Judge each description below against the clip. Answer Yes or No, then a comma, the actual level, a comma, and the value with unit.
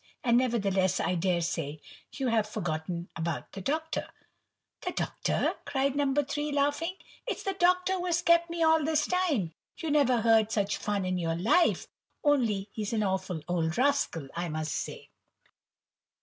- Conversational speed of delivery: Yes, average, 155 wpm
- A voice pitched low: No, high, 230 Hz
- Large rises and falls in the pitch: Yes, wide, 8.6 semitones